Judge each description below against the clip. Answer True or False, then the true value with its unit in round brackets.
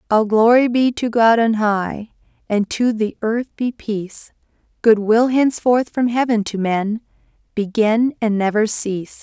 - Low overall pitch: False (225 Hz)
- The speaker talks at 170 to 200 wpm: False (155 wpm)